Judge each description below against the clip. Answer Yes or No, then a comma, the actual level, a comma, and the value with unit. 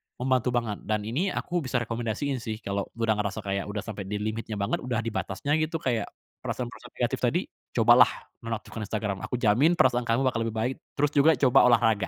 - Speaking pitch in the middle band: No, low, 115 Hz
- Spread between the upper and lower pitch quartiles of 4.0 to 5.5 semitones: No, average, 3.1 semitones